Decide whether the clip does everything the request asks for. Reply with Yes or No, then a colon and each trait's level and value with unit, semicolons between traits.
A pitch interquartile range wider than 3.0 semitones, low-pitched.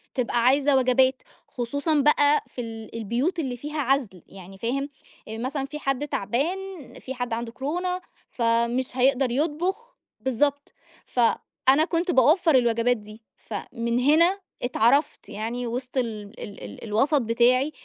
No: average, 3.8 semitones; very high, 255 Hz